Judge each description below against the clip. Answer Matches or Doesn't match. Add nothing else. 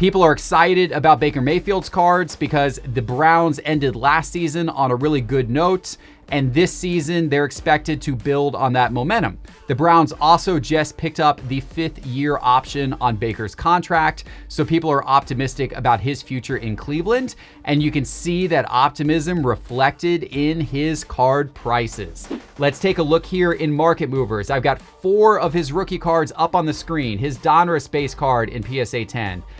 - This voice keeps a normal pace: Matches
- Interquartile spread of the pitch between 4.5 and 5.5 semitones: Doesn't match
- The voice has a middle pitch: Matches